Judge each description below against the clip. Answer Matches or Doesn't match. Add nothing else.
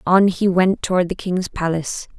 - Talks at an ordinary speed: Matches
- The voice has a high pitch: Doesn't match